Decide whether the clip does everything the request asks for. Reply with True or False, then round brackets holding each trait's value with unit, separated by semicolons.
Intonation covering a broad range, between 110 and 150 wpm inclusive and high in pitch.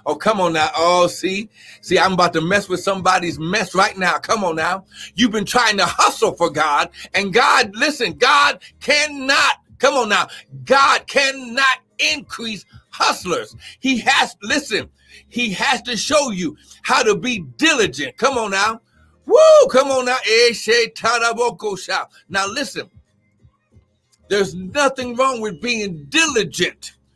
True (6.7 semitones; 145 wpm; 220 Hz)